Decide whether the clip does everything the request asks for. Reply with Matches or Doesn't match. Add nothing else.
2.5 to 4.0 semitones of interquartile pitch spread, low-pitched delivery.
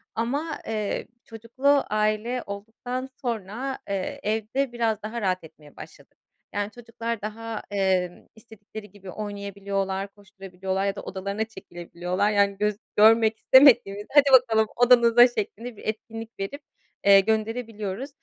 Doesn't match